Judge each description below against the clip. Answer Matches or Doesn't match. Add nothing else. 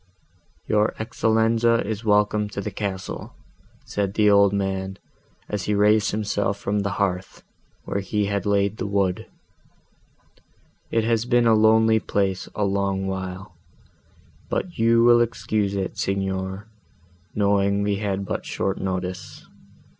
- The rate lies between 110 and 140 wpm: Matches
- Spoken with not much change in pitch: Matches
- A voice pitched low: Matches